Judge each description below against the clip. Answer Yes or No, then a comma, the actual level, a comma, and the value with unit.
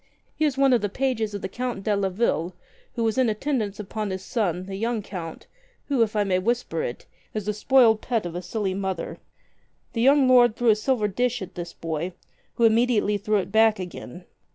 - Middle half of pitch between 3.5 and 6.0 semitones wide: Yes, average, 4.1 semitones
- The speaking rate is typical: No, fast, 215 wpm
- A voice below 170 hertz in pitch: No, high, 210 Hz